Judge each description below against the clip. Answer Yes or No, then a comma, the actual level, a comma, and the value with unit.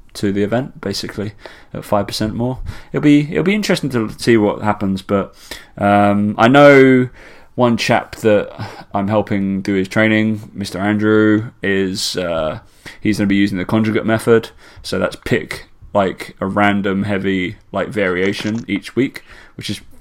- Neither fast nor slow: Yes, average, 160 wpm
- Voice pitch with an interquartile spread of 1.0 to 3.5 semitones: Yes, narrow, 2.5 semitones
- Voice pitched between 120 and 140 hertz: No, low, 105 Hz